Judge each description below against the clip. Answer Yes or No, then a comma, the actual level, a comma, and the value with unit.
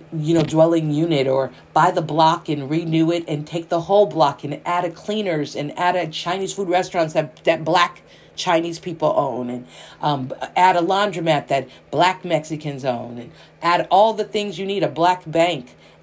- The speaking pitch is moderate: Yes, medium, 165 Hz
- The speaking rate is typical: Yes, average, 190 wpm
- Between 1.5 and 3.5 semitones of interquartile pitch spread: Yes, average, 3.2 semitones